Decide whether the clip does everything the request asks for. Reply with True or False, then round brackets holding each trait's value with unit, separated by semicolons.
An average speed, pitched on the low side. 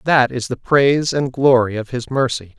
False (210 wpm; 125 Hz)